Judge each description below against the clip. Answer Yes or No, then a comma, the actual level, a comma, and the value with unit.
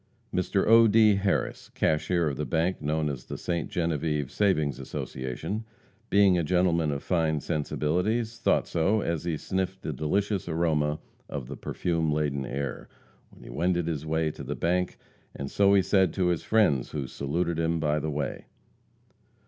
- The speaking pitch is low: Yes, very low, 80 Hz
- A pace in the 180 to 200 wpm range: No, average, 170 wpm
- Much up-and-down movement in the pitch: No, average, 3.7 semitones